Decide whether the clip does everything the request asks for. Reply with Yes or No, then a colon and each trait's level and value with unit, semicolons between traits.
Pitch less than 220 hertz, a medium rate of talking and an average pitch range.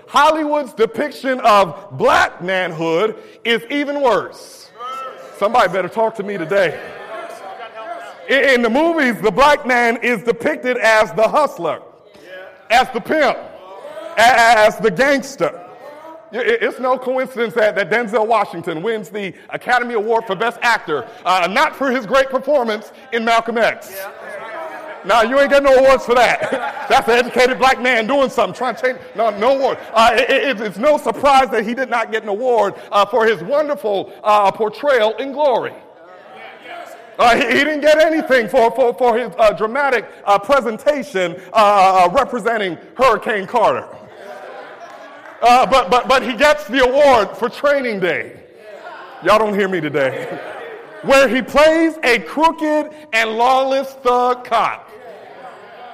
No: high, 245 Hz; average, 150 wpm; average, 4.1 semitones